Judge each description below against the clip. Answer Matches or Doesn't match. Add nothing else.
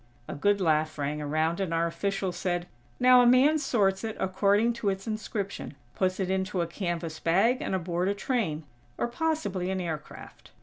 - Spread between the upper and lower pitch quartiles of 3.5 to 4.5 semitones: Matches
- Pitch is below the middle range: Doesn't match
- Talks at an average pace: Matches